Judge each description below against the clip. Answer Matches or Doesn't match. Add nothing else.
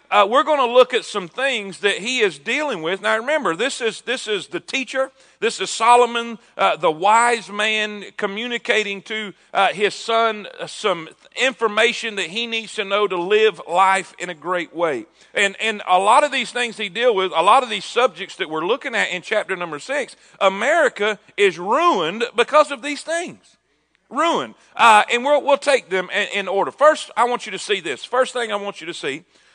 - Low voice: Doesn't match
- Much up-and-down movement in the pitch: Doesn't match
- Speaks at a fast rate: Matches